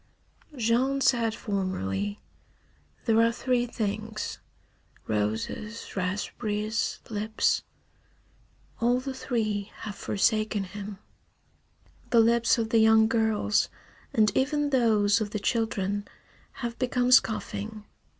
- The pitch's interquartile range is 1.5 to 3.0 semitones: Yes, narrow, 2.4 semitones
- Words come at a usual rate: No, slow, 100 wpm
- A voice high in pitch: Yes, high, 220 Hz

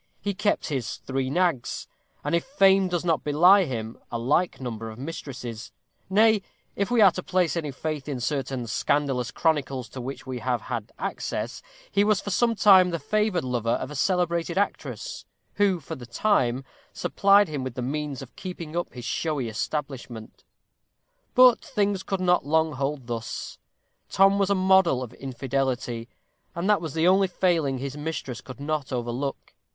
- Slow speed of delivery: No, average, 175 wpm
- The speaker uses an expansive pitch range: Yes, wide, 6.3 semitones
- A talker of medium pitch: Yes, medium, 150 Hz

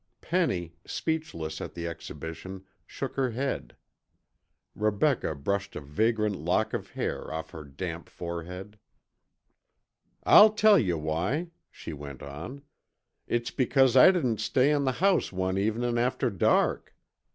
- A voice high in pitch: No, low, 105 Hz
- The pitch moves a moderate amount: No, wide, 7.9 semitones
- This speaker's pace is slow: Yes, slow, 130 wpm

